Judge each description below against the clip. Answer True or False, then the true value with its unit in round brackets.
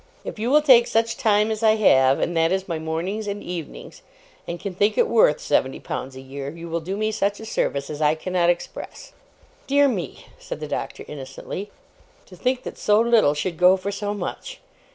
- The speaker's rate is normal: False (210 wpm)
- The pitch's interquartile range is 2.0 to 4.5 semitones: False (5.2 semitones)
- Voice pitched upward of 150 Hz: True (190 Hz)